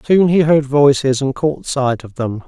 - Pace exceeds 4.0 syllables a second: Yes, 4.3 syllables/s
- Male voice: Yes, male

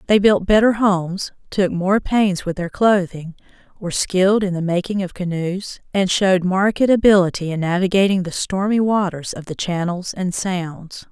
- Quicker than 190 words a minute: No, average, 165 wpm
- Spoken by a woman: Yes, female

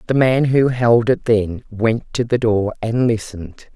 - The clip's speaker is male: No, female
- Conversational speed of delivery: Yes, average, 190 wpm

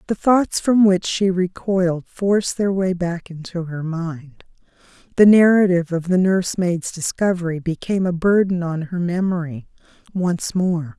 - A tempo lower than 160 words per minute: Yes, average, 145 wpm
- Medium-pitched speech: Yes, medium, 180 Hz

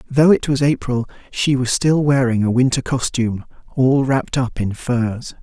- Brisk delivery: No, average, 175 wpm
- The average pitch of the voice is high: No, low, 130 Hz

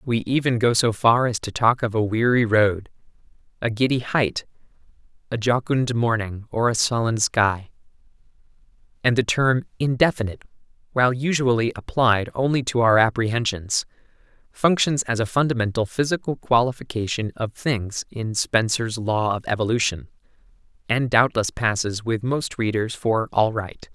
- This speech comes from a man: Yes, male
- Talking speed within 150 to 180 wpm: No, average, 140 wpm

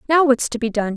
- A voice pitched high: Yes, very high, 250 Hz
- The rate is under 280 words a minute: No, fast, 315 wpm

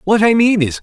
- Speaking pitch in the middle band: No, high, 205 Hz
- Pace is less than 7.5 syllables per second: Yes, 5.6 syllables/s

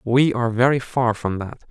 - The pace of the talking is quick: Yes, fast, 210 wpm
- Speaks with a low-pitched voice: Yes, low, 120 Hz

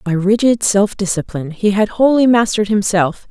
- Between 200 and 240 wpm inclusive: No, average, 165 wpm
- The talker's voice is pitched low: No, high, 205 Hz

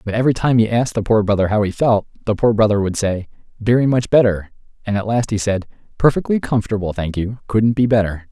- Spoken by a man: Yes, male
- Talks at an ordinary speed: No, fast, 225 wpm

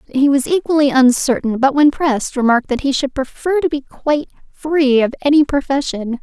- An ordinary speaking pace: Yes, average, 185 wpm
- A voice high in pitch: Yes, very high, 275 Hz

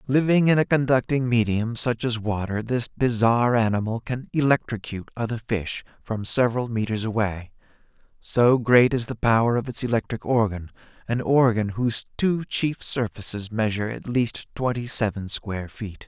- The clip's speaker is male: Yes, male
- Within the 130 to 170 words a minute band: Yes, average, 155 wpm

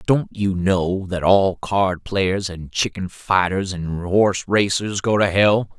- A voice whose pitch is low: Yes, very low, 95 Hz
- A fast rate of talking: No, average, 165 wpm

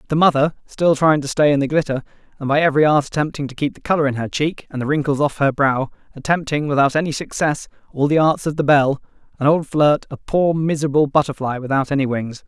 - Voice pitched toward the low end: No, medium, 145 Hz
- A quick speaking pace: Yes, fast, 220 wpm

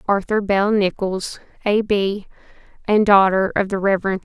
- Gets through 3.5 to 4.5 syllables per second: Yes, 4.2 syllables/s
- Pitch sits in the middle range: No, high, 200 Hz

